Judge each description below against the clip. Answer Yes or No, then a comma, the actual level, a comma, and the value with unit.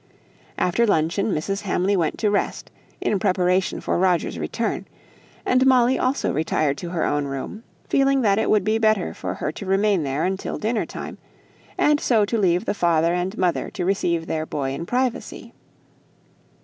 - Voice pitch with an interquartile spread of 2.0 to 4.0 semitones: No, average, 4.6 semitones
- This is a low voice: No, high, 190 Hz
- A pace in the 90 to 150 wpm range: No, average, 175 wpm